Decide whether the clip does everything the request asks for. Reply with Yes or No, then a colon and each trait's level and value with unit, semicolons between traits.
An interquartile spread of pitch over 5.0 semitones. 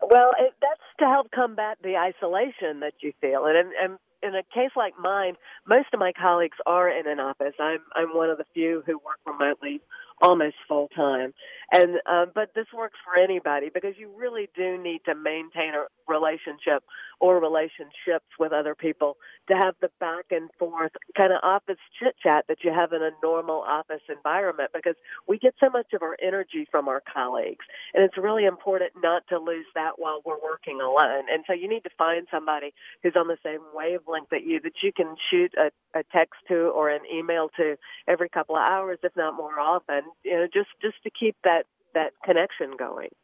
No: average, 3.5 semitones